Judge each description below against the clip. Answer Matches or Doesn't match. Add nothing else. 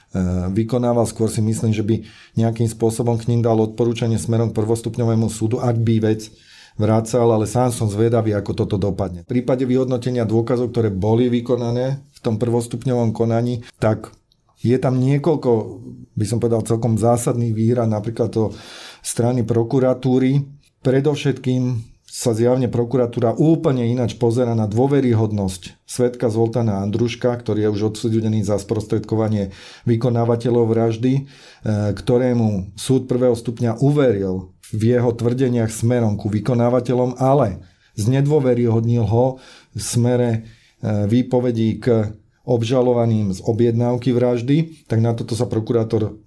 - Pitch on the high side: Doesn't match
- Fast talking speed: Doesn't match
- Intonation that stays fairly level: Matches